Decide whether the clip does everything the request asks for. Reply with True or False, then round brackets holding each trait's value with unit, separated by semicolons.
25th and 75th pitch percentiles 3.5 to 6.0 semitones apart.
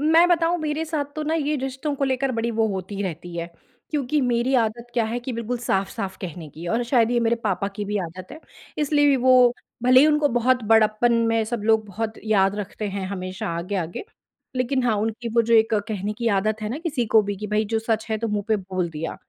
True (4.0 semitones)